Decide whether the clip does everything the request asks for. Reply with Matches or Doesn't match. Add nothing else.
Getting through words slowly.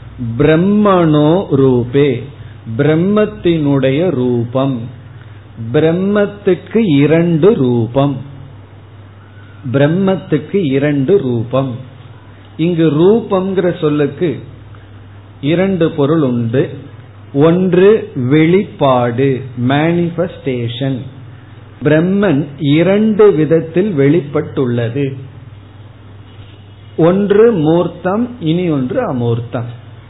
Matches